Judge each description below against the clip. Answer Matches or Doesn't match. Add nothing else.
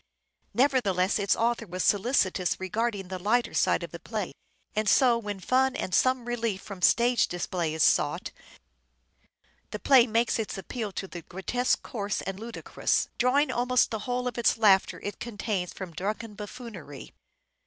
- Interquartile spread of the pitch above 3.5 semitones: Matches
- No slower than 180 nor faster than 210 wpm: Doesn't match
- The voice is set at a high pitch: Matches